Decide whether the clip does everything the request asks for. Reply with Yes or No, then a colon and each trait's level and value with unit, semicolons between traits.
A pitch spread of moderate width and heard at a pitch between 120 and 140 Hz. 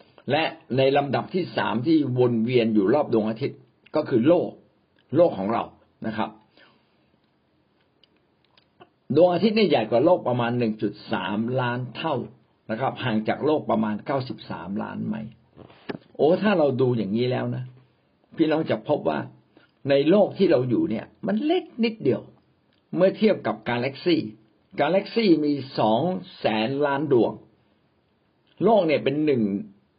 No: wide, 6.2 semitones; low, 130 Hz